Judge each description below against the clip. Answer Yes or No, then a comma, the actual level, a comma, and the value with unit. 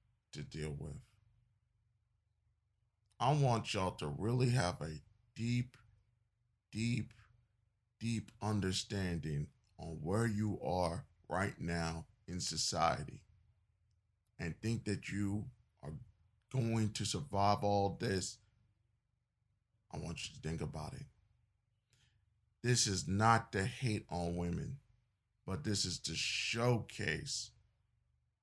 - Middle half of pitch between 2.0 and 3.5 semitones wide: Yes, average, 2.8 semitones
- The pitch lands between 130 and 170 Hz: No, low, 110 Hz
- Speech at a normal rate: No, slow, 110 wpm